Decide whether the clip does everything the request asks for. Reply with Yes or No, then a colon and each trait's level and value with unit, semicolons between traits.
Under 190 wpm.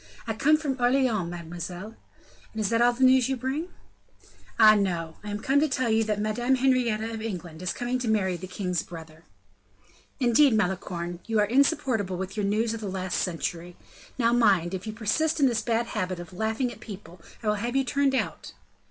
No: fast, 205 wpm